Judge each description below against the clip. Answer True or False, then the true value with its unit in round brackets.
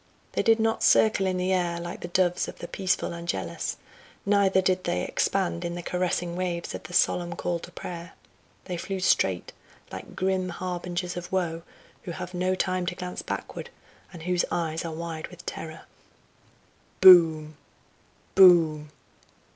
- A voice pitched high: False (175 Hz)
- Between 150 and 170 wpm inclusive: True (160 wpm)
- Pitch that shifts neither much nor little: False (1.5 semitones)